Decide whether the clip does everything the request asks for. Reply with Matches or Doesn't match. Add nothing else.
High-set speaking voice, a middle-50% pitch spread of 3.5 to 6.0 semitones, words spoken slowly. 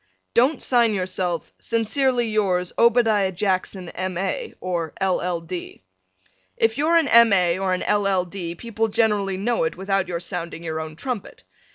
Doesn't match